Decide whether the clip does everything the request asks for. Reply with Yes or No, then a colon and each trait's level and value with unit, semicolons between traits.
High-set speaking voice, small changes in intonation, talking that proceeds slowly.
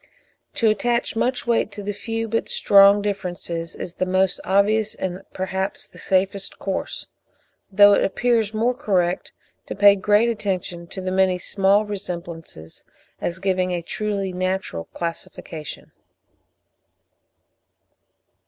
Yes: high, 195 Hz; narrow, 2.3 semitones; slow, 125 wpm